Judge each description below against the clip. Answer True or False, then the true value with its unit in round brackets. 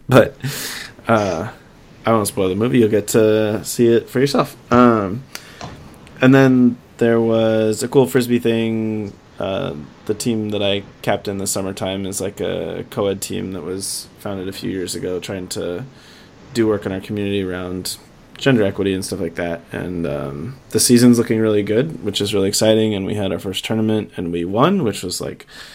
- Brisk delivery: False (190 wpm)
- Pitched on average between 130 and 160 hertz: False (105 Hz)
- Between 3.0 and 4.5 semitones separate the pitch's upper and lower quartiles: True (3.3 semitones)